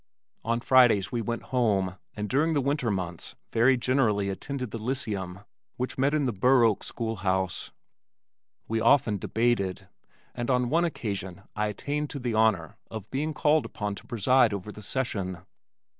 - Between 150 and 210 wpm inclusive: Yes, average, 165 wpm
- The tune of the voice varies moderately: Yes, average, 4.6 semitones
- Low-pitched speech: Yes, low, 115 Hz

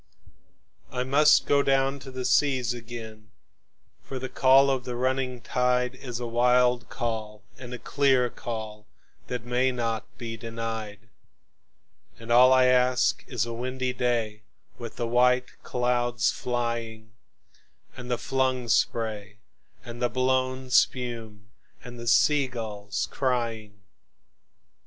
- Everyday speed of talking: No, slow, 130 wpm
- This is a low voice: Yes, low, 125 Hz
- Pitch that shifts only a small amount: Yes, narrow, 2.0 semitones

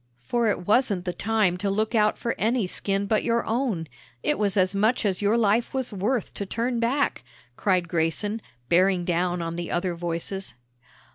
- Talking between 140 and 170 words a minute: No, average, 185 wpm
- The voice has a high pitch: Yes, high, 200 Hz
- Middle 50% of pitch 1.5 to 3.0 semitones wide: No, average, 4.1 semitones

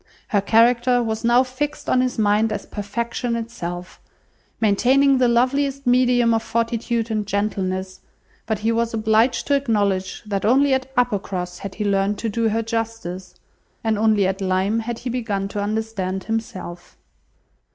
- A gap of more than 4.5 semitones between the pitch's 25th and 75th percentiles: No, average, 3.0 semitones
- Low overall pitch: No, high, 225 Hz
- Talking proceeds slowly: No, average, 155 wpm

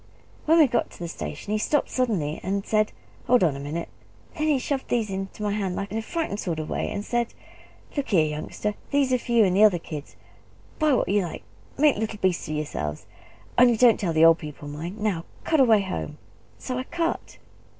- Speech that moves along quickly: Yes, fast, 215 wpm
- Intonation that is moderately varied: No, wide, 6.7 semitones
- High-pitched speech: Yes, high, 210 Hz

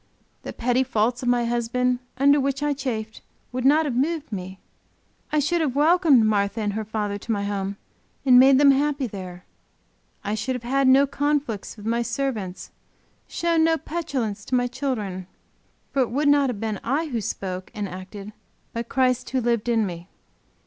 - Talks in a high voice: Yes, high, 245 Hz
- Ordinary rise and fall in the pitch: Yes, average, 4.6 semitones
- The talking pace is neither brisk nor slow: Yes, average, 185 wpm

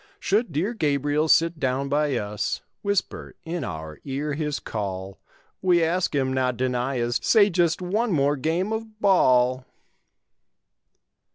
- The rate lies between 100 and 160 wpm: Yes, slow, 135 wpm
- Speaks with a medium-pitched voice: Yes, medium, 150 Hz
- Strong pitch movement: Yes, wide, 5.8 semitones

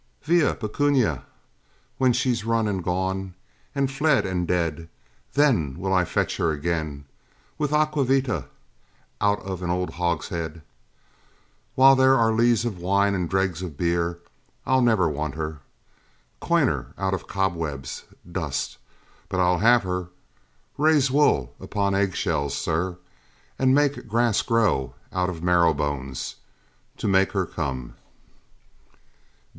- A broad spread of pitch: Yes, wide, 6.0 semitones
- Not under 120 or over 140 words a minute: Yes, slow, 135 wpm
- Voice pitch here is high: No, very low, 95 Hz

